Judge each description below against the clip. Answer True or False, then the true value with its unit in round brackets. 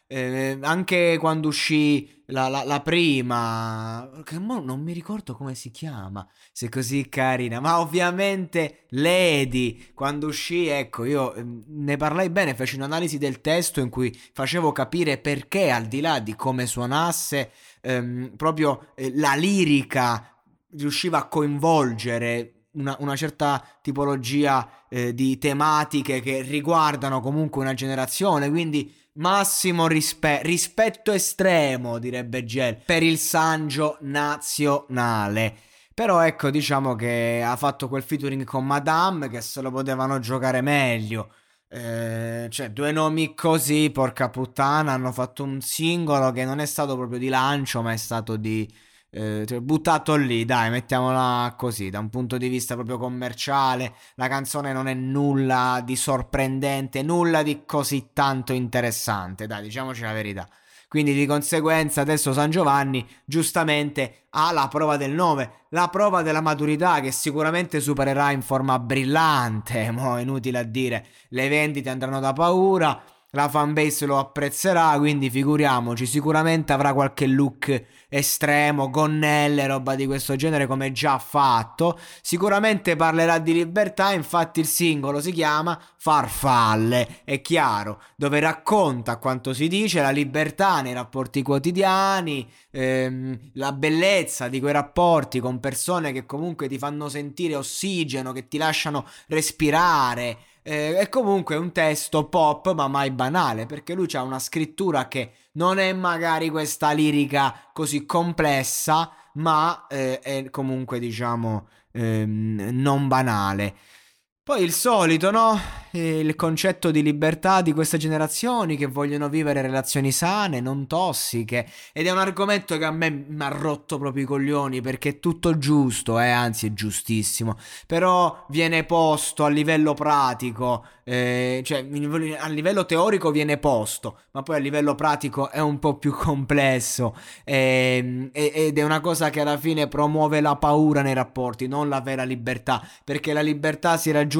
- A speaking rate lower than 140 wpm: False (145 wpm)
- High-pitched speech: False (140 Hz)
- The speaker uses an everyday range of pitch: True (3.4 semitones)